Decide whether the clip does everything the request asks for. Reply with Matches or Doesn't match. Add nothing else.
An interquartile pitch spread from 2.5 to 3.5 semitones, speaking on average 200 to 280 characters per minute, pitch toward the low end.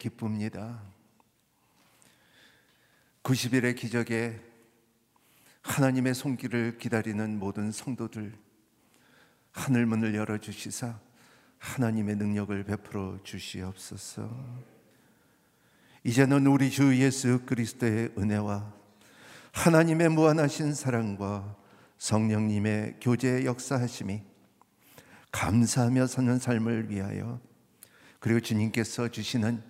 Matches